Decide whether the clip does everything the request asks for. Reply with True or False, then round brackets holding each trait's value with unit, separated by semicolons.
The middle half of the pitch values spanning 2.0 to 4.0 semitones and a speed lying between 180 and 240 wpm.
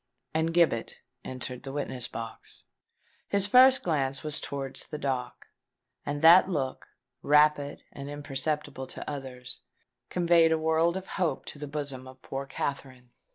False (3.4 semitones; 145 wpm)